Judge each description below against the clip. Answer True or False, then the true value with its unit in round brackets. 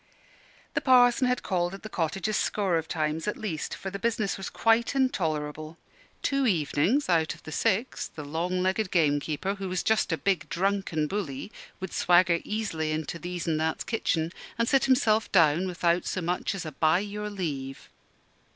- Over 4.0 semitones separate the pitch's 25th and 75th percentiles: True (4.7 semitones)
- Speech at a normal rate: True (180 wpm)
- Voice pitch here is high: False (180 Hz)